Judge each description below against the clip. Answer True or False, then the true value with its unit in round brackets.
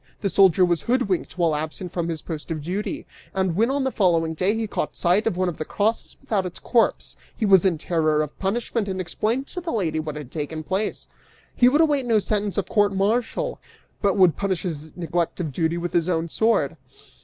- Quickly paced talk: True (215 wpm)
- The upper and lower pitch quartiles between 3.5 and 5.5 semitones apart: True (4.5 semitones)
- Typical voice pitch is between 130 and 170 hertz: False (185 Hz)